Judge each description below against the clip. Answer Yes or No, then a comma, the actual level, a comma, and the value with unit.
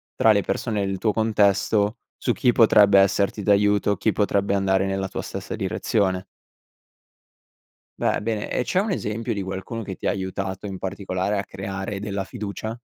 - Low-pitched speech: Yes, low, 100 Hz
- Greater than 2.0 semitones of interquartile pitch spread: No, narrow, 1.7 semitones